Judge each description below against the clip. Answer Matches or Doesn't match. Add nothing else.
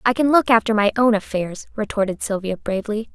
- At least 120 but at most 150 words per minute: Doesn't match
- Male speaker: Doesn't match